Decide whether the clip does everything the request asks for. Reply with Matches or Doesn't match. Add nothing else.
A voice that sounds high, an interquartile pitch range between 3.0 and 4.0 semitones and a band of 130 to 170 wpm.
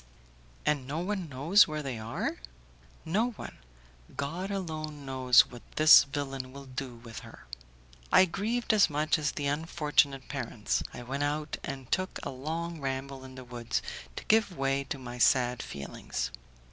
Doesn't match